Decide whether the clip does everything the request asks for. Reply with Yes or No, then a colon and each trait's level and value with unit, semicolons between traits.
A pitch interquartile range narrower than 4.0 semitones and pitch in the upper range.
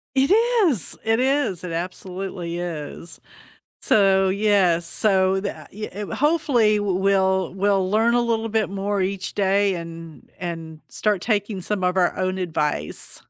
Yes: average, 2.8 semitones; high, 195 Hz